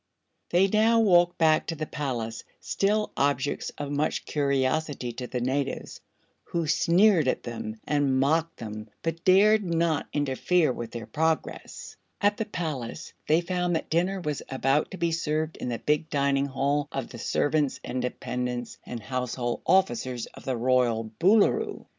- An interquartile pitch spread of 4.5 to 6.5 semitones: Yes, average, 4.9 semitones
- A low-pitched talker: No, medium, 145 Hz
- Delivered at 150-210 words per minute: Yes, average, 160 wpm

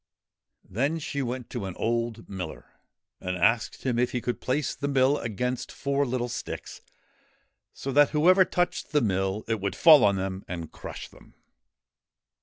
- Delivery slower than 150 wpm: No, average, 165 wpm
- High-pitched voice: No, low, 120 Hz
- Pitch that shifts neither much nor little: No, wide, 5.7 semitones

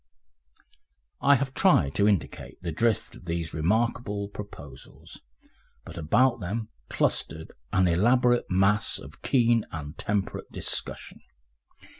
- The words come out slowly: Yes, slow, 115 wpm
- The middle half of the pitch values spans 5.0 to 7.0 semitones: Yes, wide, 5.6 semitones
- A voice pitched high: No, low, 105 Hz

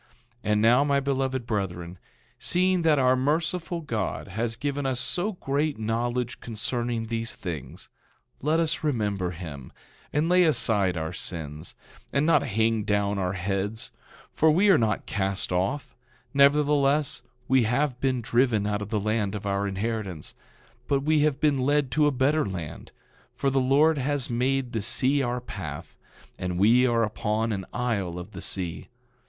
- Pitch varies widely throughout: Yes, wide, 5.8 semitones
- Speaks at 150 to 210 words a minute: Yes, average, 165 wpm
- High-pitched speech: No, low, 120 Hz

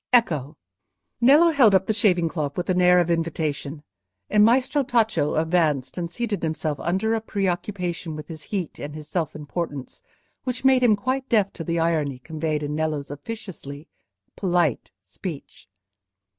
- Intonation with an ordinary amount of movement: No, wide, 5.7 semitones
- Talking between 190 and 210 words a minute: No, average, 155 wpm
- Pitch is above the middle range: No, medium, 170 Hz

